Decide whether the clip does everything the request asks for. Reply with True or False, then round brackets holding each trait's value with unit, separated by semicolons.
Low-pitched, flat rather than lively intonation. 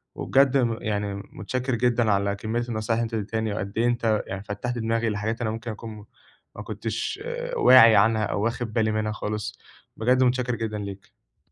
True (110 Hz; 2.3 semitones)